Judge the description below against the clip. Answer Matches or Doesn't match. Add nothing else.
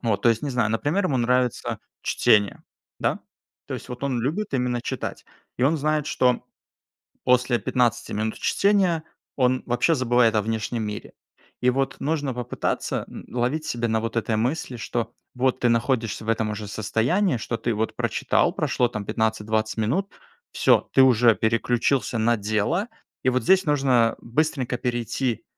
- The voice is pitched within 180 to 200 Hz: Doesn't match